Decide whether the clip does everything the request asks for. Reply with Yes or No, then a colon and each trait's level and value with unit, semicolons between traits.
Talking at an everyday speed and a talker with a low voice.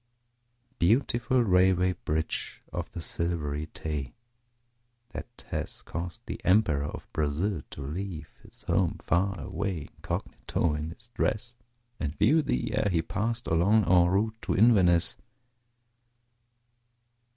No: slow, 120 wpm; very low, 90 Hz